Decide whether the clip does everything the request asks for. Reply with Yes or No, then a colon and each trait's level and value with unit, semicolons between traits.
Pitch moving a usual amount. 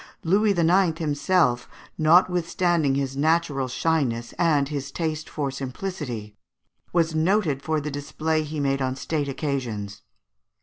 Yes: average, 3.4 semitones